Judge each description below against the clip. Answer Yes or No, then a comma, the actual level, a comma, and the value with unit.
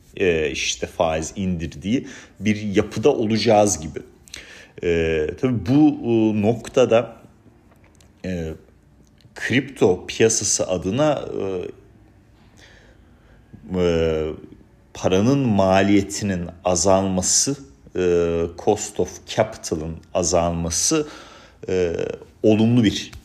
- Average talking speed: No, slow, 70 wpm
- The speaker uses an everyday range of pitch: Yes, average, 4.7 semitones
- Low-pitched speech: Yes, very low, 95 Hz